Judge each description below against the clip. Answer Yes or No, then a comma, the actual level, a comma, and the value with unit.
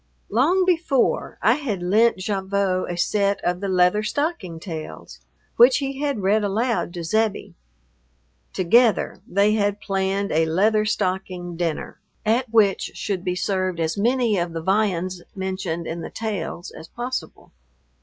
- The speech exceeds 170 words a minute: No, average, 145 wpm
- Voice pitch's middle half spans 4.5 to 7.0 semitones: No, average, 3.7 semitones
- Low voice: No, high, 200 Hz